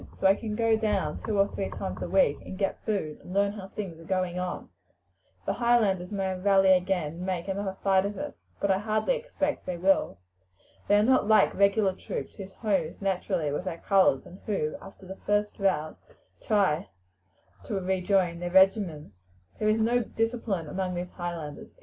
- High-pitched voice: Yes, high, 195 Hz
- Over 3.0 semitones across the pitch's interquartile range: No, narrow, 2.5 semitones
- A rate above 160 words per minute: Yes, average, 190 wpm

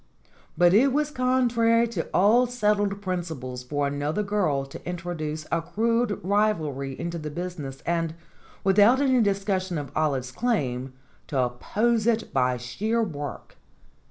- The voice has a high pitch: No, medium, 180 Hz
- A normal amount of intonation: No, wide, 7.3 semitones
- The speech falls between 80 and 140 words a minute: Yes, slow, 135 wpm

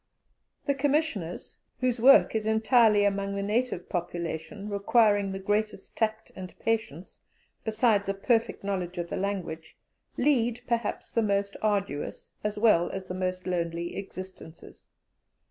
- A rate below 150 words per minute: Yes, slow, 135 wpm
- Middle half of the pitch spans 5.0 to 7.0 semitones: No, average, 3.4 semitones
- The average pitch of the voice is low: No, high, 200 Hz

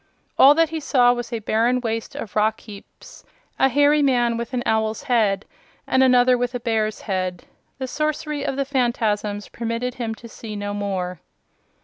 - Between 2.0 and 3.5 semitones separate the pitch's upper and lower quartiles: Yes, average, 3.2 semitones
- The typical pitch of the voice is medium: No, high, 235 Hz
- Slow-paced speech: No, average, 175 wpm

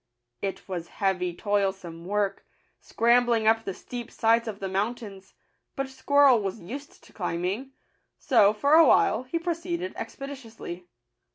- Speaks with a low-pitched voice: No, high, 225 Hz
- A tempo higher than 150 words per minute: No, slow, 135 wpm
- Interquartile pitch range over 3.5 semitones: Yes, wide, 5.5 semitones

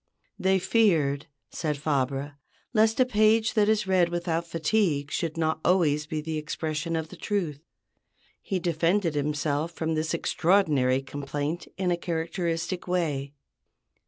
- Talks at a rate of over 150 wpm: No, slow, 135 wpm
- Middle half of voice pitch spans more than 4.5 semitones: No, average, 3.6 semitones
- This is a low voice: No, medium, 165 Hz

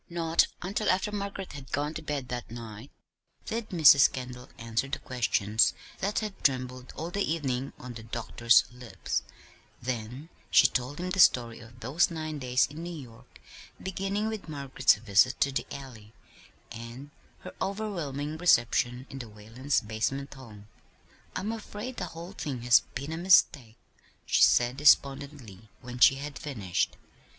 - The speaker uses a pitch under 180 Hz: Yes, low, 135 Hz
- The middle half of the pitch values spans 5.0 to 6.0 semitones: Yes, wide, 5.4 semitones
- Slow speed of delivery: No, average, 155 wpm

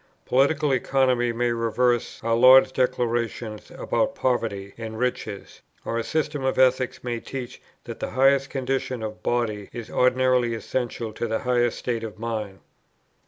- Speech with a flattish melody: Yes, narrow, 2.1 semitones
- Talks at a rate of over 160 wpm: No, average, 150 wpm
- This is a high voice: No, low, 120 Hz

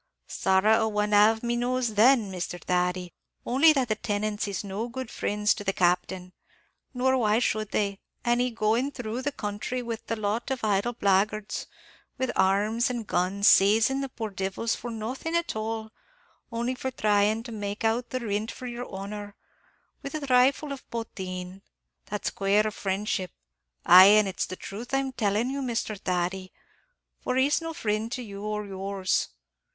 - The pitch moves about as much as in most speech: Yes, average, 3.4 semitones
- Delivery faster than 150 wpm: Yes, average, 170 wpm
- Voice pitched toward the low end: No, high, 215 Hz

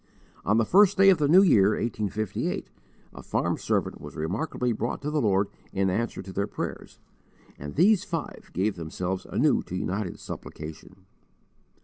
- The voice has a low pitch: Yes, low, 105 Hz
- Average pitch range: No, wide, 8.0 semitones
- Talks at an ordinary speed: Yes, average, 160 wpm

